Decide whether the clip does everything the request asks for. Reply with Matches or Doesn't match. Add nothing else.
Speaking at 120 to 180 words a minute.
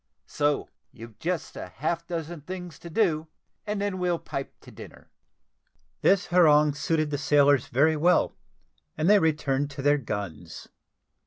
Matches